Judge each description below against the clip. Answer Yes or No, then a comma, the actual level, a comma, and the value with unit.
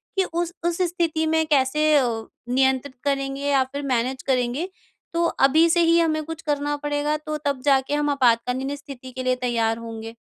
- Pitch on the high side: Yes, very high, 280 Hz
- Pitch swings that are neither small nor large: Yes, average, 3.4 semitones